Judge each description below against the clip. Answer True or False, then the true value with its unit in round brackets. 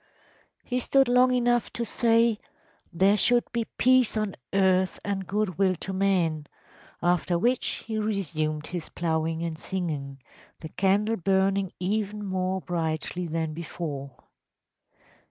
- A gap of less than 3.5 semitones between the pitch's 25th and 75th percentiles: False (4.4 semitones)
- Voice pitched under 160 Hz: False (190 Hz)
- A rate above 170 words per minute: False (135 wpm)